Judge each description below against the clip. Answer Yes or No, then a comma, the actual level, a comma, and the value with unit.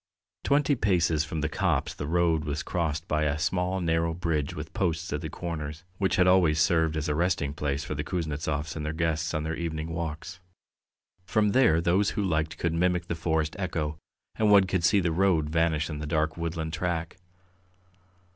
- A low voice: Yes, very low, 80 Hz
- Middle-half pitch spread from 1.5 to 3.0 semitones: Yes, narrow, 2.4 semitones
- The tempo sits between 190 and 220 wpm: Yes, average, 195 wpm